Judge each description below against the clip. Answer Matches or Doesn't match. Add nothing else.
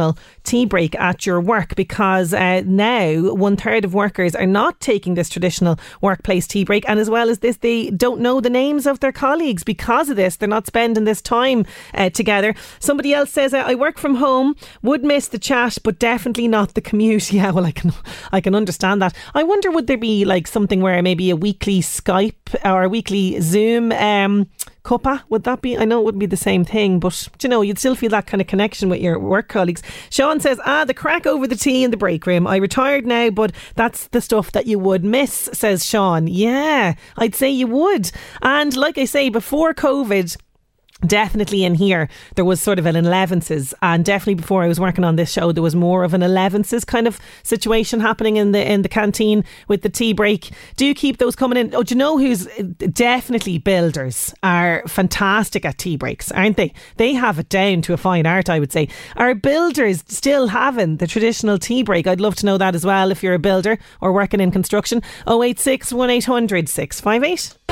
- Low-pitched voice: Doesn't match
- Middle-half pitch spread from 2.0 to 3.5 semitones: Doesn't match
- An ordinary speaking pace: Doesn't match